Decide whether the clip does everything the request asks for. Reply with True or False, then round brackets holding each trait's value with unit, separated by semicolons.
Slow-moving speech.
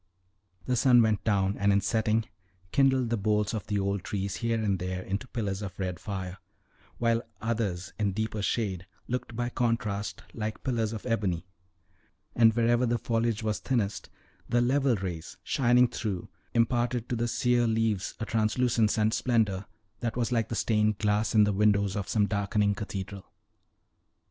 False (165 wpm)